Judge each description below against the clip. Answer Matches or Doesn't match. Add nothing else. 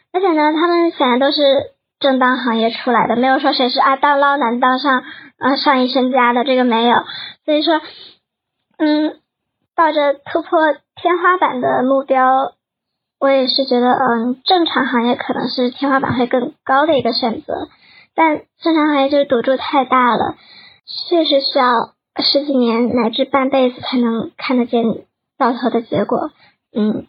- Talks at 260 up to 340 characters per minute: Doesn't match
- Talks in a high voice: Matches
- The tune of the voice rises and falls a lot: Doesn't match